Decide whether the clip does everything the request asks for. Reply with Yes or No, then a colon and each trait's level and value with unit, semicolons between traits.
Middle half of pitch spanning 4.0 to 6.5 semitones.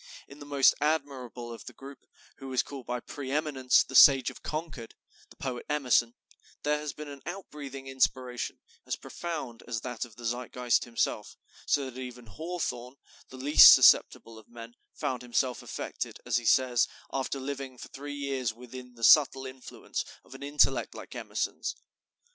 No: narrow, 2.6 semitones